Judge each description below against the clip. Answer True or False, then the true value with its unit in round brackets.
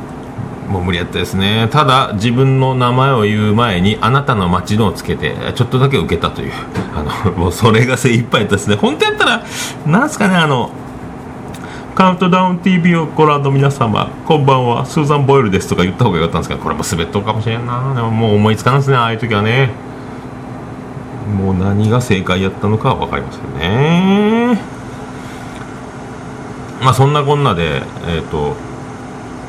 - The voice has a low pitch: True (120 Hz)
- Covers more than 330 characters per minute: True (370 characters per minute)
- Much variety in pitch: False (4.9 semitones)